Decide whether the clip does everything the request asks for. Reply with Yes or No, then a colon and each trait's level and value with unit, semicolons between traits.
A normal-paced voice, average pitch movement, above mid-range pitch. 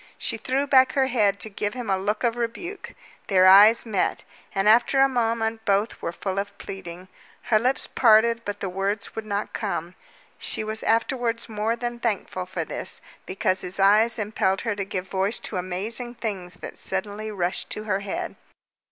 Yes: average, 185 wpm; average, 3.1 semitones; high, 215 Hz